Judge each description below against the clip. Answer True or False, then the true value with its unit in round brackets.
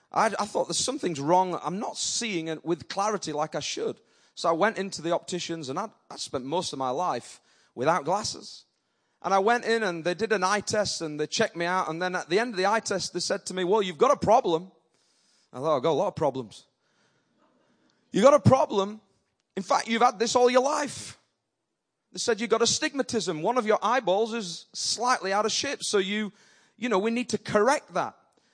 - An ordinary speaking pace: False (225 wpm)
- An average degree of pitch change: True (4.5 semitones)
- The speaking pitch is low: False (205 Hz)